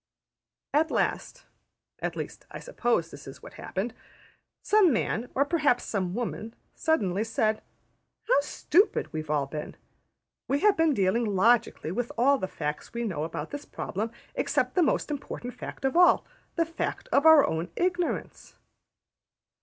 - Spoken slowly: No, average, 155 wpm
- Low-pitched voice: No, high, 240 Hz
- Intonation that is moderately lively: No, wide, 8.8 semitones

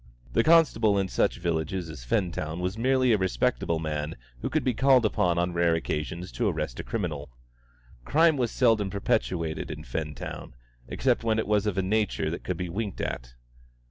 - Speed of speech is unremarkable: Yes, average, 180 wpm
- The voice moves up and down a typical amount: No, wide, 5.8 semitones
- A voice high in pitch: No, very low, 95 Hz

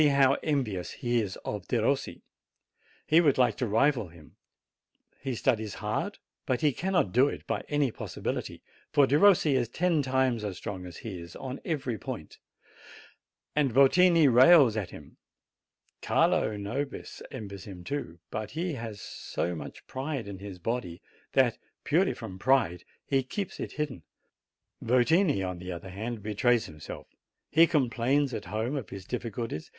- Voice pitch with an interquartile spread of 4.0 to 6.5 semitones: Yes, wide, 5.6 semitones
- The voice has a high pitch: No, low, 125 Hz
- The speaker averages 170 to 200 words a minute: No, average, 155 wpm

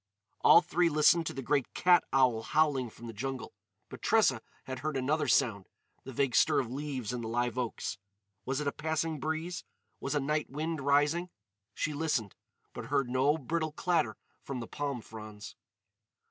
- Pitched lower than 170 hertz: Yes, medium, 140 Hz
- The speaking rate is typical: Yes, average, 175 wpm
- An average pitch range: Yes, average, 3.9 semitones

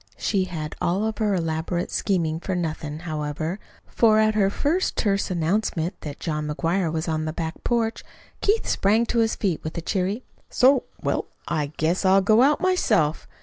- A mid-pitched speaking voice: Yes, medium, 180 Hz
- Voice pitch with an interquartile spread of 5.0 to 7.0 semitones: Yes, average, 5.3 semitones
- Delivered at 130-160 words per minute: No, average, 180 wpm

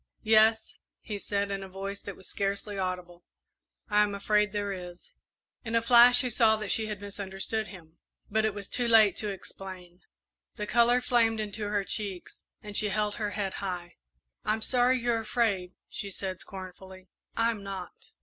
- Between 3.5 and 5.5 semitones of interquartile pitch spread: No, narrow, 2.4 semitones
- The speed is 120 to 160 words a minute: No, average, 175 wpm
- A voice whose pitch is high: Yes, high, 205 Hz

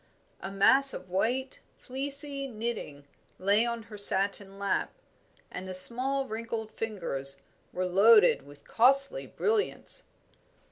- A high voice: Yes, high, 220 Hz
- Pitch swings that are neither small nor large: No, wide, 5.7 semitones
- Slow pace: Yes, slow, 120 wpm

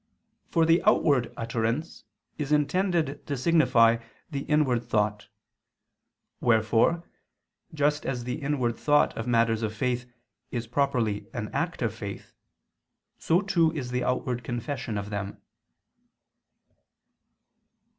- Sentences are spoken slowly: Yes, slow, 115 wpm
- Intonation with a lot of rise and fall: No, average, 4.5 semitones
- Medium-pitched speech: No, low, 125 Hz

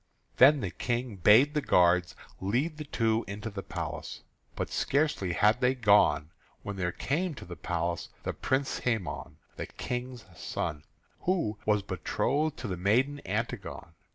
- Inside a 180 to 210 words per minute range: No, average, 155 wpm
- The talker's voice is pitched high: No, low, 110 Hz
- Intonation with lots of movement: Yes, wide, 5.9 semitones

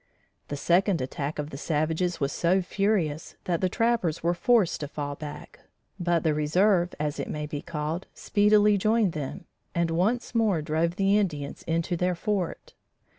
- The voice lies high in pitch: No, medium, 170 Hz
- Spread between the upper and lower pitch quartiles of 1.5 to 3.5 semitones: No, average, 4.4 semitones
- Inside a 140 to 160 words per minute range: No, average, 170 wpm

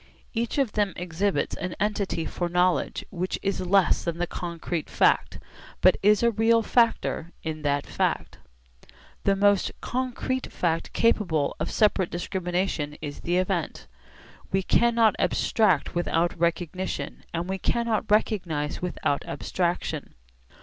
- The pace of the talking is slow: Yes, slow, 130 wpm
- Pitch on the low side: No, medium, 185 Hz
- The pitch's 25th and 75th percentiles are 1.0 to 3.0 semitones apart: No, average, 3.7 semitones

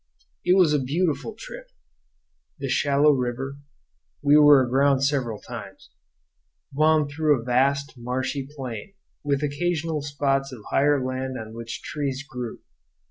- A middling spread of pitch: No, narrow, 2.3 semitones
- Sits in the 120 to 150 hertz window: Yes, medium, 140 Hz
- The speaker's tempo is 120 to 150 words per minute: Yes, slow, 135 wpm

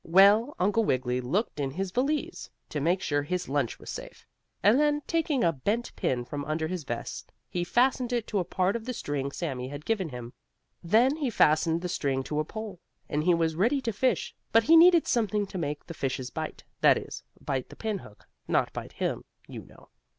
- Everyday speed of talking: No, fast, 210 wpm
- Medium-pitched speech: Yes, medium, 180 Hz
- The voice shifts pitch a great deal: Yes, wide, 7.8 semitones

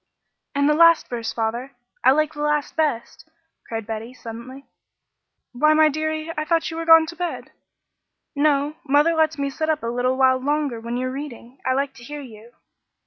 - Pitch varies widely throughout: No, average, 3.9 semitones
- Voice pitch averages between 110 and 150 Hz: No, very high, 280 Hz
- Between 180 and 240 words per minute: Yes, average, 190 wpm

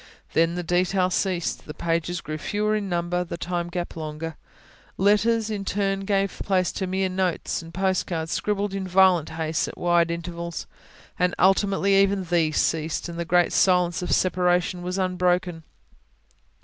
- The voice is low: No, medium, 180 Hz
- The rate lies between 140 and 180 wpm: Yes, average, 160 wpm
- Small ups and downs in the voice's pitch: Yes, narrow, 2.2 semitones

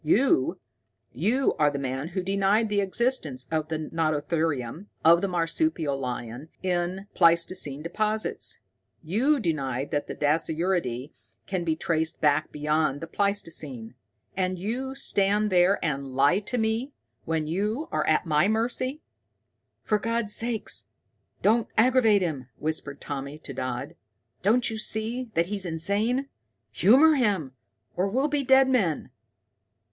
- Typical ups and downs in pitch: No, wide, 6.2 semitones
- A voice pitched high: No, medium, 180 Hz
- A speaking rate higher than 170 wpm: No, slow, 135 wpm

